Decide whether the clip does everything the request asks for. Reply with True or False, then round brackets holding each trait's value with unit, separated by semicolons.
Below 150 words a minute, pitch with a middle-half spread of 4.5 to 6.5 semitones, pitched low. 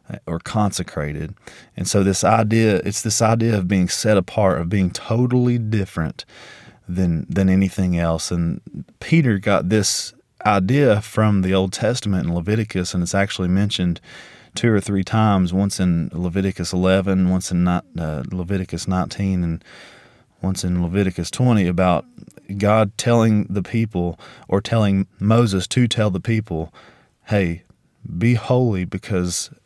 False (140 wpm; 3.3 semitones; 100 Hz)